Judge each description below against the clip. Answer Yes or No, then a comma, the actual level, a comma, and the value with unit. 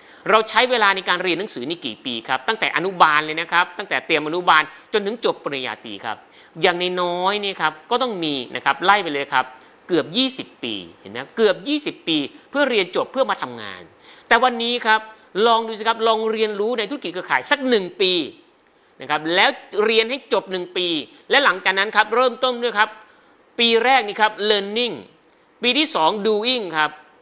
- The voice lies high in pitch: Yes, high, 215 Hz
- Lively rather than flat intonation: Yes, wide, 6.1 semitones